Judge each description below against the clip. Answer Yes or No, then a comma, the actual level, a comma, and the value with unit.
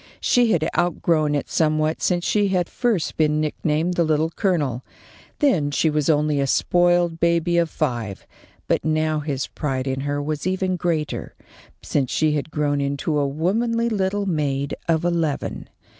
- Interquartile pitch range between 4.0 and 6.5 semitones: No, average, 3.2 semitones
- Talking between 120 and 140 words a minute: No, average, 160 wpm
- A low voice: No, medium, 155 Hz